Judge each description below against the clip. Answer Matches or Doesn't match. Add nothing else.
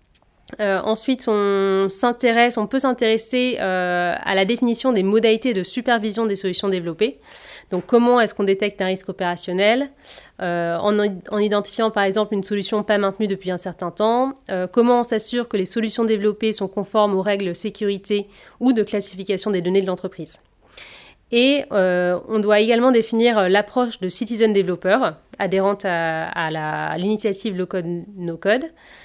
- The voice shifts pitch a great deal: Doesn't match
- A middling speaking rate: Matches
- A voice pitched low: Doesn't match